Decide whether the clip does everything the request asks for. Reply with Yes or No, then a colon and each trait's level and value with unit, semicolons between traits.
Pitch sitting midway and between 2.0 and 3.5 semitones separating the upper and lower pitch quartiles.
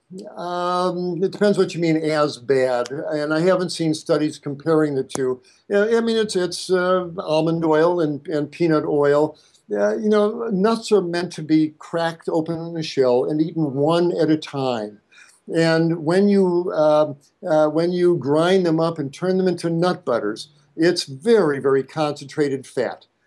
Yes: medium, 165 Hz; average, 3.2 semitones